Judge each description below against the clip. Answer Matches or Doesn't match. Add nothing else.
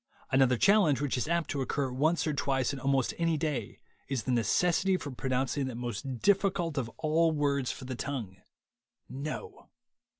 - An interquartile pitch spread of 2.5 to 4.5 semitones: Matches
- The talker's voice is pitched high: Doesn't match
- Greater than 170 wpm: Matches